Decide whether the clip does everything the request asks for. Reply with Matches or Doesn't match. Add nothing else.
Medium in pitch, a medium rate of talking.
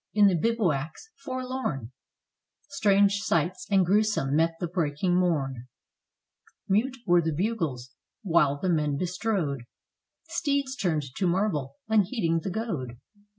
Doesn't match